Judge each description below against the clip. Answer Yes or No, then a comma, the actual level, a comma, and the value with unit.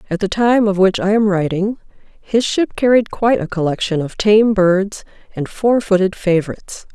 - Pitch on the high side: Yes, high, 200 Hz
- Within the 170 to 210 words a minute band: Yes, average, 180 wpm